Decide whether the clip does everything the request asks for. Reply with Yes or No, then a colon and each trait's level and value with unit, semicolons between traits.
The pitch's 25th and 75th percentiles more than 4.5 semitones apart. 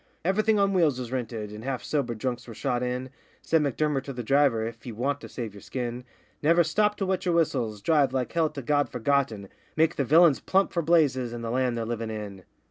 Yes: average, 4.9 semitones